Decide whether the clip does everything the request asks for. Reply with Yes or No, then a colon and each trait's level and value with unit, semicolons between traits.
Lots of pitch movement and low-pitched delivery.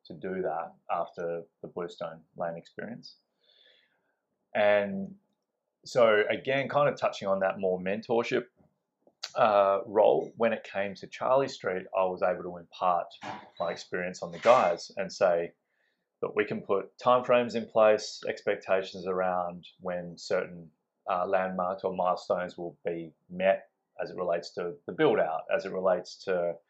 No: average, 3.8 semitones; very low, 95 Hz